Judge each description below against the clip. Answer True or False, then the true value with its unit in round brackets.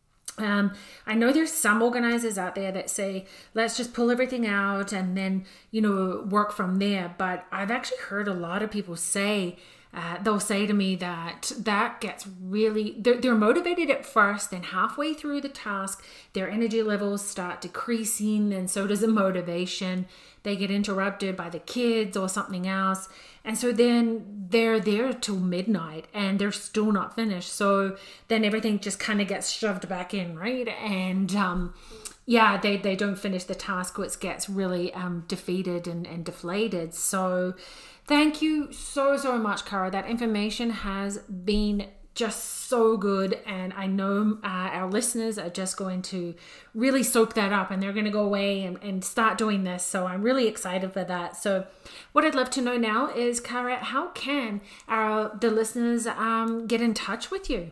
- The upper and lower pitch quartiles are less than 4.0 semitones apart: True (3.1 semitones)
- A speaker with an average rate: True (180 wpm)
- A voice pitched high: True (205 Hz)